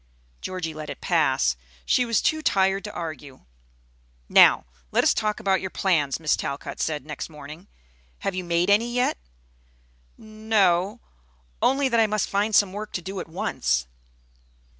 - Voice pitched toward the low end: No, high, 190 Hz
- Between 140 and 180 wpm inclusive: Yes, average, 160 wpm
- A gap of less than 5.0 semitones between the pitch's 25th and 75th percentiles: No, wide, 5.4 semitones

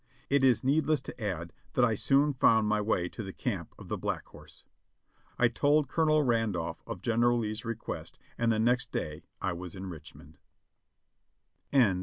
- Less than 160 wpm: No, average, 170 wpm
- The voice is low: Yes, low, 115 Hz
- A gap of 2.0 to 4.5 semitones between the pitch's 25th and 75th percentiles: No, wide, 5.4 semitones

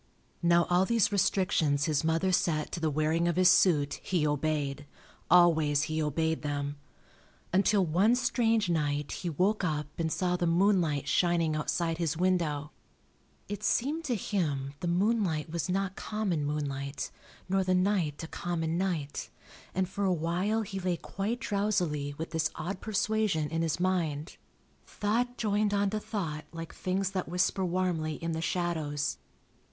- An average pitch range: Yes, average, 3.9 semitones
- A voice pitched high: No, medium, 175 Hz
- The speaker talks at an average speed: Yes, average, 155 wpm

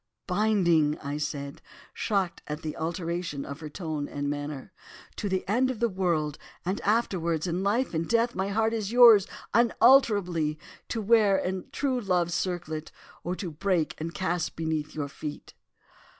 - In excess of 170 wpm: No, average, 155 wpm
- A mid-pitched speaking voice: Yes, medium, 180 Hz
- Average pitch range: Yes, average, 4.9 semitones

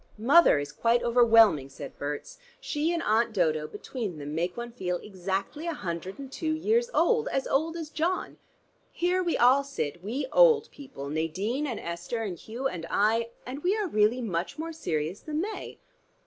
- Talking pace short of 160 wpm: No, average, 180 wpm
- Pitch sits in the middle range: No, high, 235 Hz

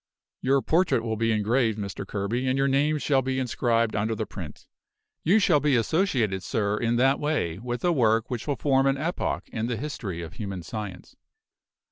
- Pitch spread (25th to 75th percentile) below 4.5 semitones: Yes, average, 4.1 semitones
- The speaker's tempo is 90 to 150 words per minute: No, average, 190 wpm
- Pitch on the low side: Yes, low, 120 Hz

